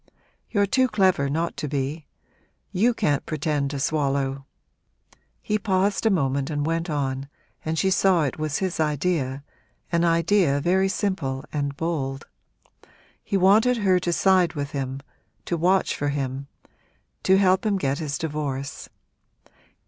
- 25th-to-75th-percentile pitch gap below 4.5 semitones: No, average, 5.1 semitones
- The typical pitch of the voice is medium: Yes, medium, 155 Hz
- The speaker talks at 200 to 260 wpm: No, average, 150 wpm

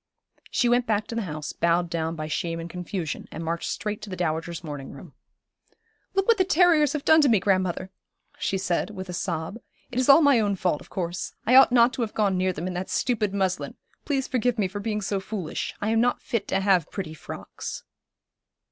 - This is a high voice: Yes, high, 195 Hz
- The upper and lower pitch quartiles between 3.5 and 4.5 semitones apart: No, wide, 5.4 semitones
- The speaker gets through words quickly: Yes, fast, 220 wpm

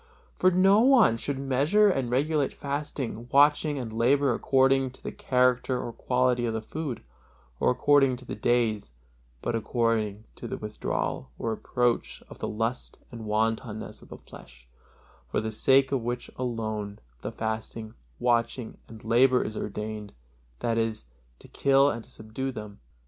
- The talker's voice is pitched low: Yes, low, 120 Hz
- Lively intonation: No, average, 3.4 semitones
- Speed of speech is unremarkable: Yes, average, 160 wpm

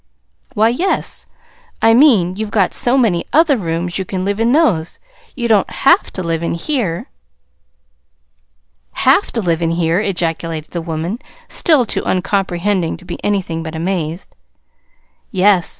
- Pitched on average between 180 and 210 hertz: Yes, high, 190 Hz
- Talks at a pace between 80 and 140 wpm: No, average, 150 wpm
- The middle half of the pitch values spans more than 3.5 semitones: Yes, average, 5.2 semitones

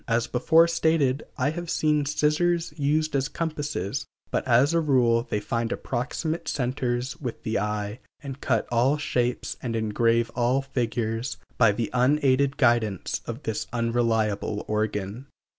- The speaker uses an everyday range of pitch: Yes, average, 4.1 semitones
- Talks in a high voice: No, low, 125 Hz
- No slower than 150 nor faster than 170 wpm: No, average, 140 wpm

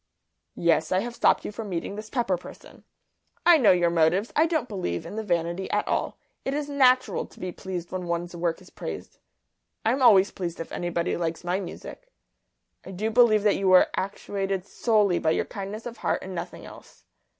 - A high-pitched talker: Yes, high, 195 Hz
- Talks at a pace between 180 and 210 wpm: Yes, average, 195 wpm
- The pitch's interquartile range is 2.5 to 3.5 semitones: No, average, 4.2 semitones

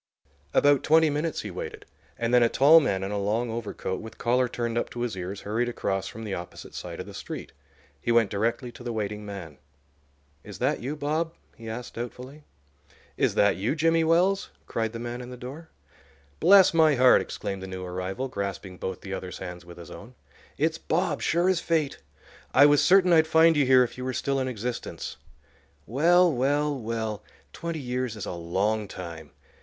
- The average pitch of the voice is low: Yes, low, 120 Hz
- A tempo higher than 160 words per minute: Yes, average, 195 wpm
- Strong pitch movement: Yes, wide, 6.4 semitones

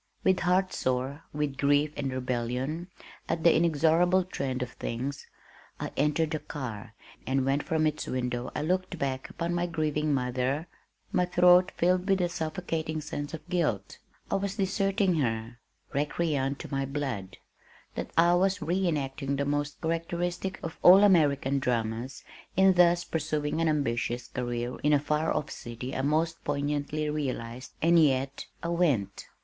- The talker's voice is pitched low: No, medium, 150 Hz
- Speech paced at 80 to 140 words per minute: No, average, 155 wpm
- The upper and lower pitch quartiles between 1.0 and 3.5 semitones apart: No, average, 4.3 semitones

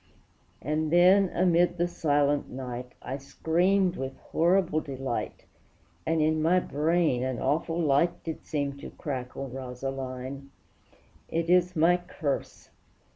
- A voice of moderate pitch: Yes, medium, 155 Hz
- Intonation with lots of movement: No, average, 4.3 semitones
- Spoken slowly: Yes, slow, 125 wpm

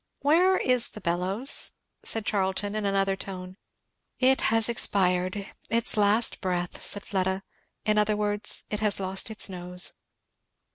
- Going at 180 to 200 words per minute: No, average, 140 wpm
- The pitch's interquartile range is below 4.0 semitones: Yes, narrow, 2.5 semitones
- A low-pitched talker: No, high, 205 Hz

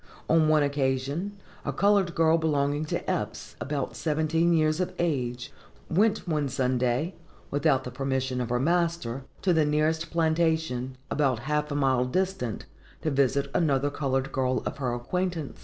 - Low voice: No, medium, 145 Hz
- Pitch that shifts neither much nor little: Yes, average, 3.7 semitones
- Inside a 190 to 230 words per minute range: No, average, 155 wpm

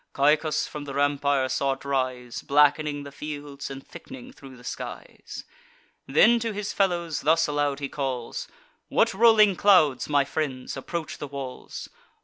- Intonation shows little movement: No, average, 3.1 semitones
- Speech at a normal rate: Yes, average, 150 wpm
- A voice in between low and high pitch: Yes, medium, 145 Hz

